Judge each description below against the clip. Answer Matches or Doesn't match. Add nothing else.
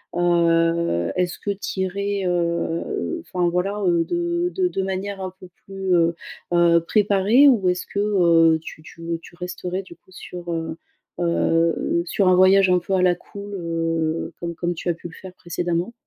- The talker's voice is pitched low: Doesn't match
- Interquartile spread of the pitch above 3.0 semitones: Doesn't match